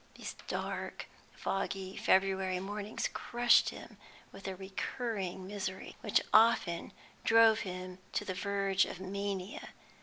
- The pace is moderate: No, slow, 120 wpm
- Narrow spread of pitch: Yes, narrow, 1.7 semitones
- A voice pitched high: Yes, high, 195 Hz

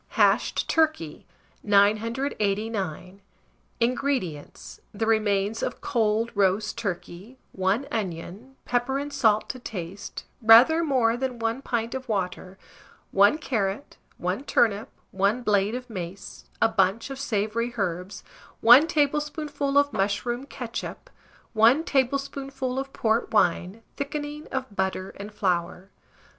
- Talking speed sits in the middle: No, slow, 120 wpm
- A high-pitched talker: Yes, high, 225 Hz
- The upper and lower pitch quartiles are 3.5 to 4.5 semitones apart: No, average, 5.0 semitones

